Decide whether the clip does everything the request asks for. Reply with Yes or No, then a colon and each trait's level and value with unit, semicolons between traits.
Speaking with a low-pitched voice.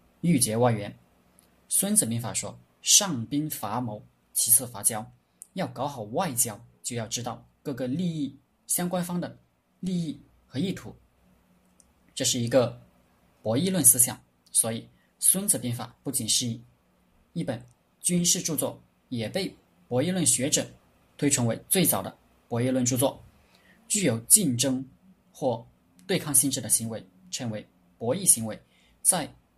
Yes: low, 120 Hz